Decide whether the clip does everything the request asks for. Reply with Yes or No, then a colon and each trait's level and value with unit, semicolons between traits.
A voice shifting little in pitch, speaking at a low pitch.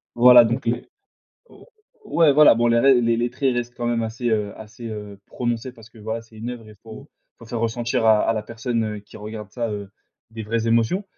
Yes: narrow, 1.6 semitones; low, 115 Hz